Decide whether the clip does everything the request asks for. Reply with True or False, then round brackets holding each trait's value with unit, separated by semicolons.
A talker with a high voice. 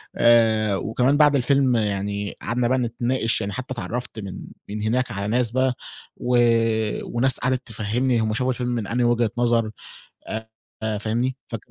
False (120 Hz)